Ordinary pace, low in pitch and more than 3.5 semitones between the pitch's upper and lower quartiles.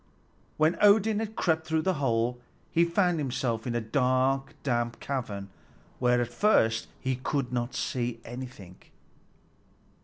No: slow, 130 wpm; low, 130 Hz; average, 5.0 semitones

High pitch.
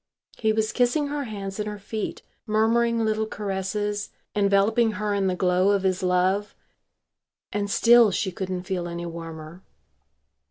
Yes: high, 205 Hz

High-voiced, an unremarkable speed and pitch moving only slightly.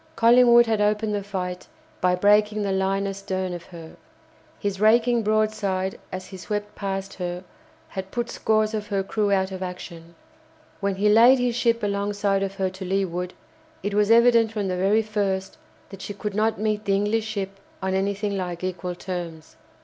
Yes: high, 200 Hz; average, 180 wpm; narrow, 2.2 semitones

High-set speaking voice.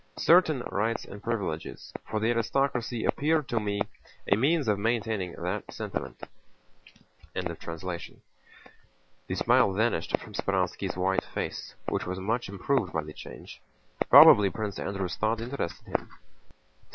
No: low, 105 Hz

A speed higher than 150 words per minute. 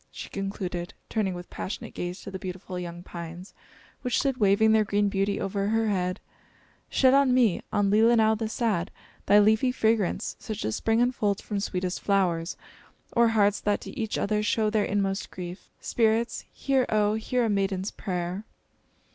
Yes: average, 170 wpm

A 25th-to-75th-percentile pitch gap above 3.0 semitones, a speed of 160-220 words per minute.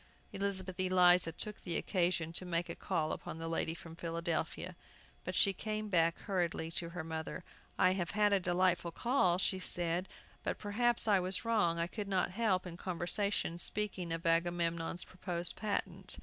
No: narrow, 2.6 semitones; average, 170 wpm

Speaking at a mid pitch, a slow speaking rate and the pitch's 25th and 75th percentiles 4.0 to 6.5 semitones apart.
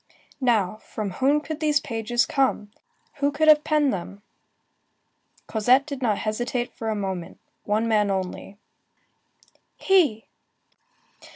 No: high, 235 Hz; slow, 115 wpm; wide, 5.4 semitones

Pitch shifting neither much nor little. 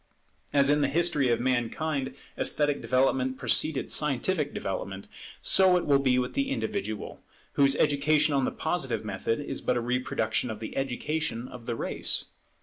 Yes: average, 3.7 semitones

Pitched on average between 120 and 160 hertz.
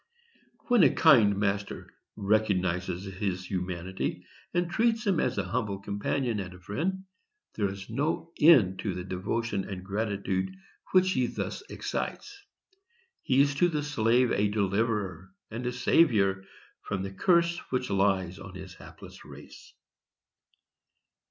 No: low, 105 Hz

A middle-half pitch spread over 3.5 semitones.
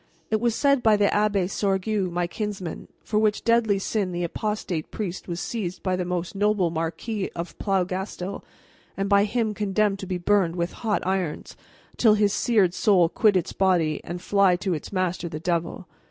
No: average, 3.0 semitones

